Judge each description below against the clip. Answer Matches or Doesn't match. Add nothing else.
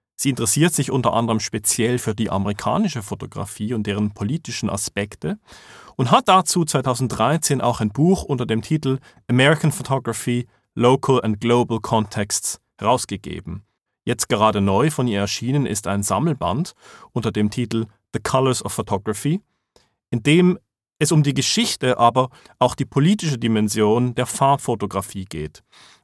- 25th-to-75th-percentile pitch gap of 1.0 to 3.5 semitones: Doesn't match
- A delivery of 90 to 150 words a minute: Matches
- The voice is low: Matches